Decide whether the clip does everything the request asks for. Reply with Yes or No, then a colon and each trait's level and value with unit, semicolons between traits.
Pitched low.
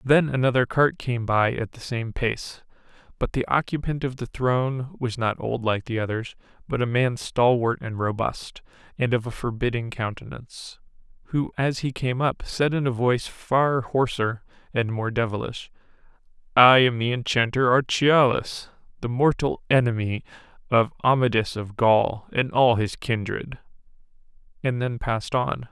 Yes: low, 120 Hz